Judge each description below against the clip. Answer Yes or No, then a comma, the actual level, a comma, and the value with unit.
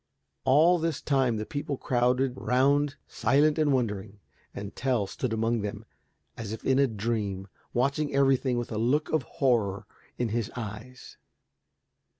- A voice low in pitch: Yes, low, 125 Hz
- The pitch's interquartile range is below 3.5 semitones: No, average, 3.8 semitones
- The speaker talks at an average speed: Yes, average, 150 wpm